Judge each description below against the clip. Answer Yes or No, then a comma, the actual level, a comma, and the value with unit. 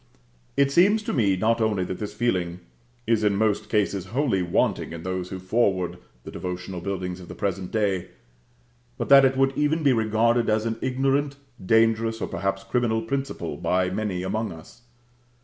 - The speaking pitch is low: Yes, low, 110 Hz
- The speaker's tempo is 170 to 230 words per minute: Yes, average, 175 wpm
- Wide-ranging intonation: No, average, 4.4 semitones